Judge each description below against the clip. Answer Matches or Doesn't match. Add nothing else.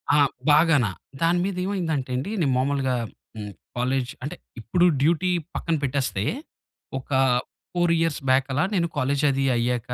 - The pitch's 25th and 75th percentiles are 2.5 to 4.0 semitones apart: Doesn't match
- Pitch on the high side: Doesn't match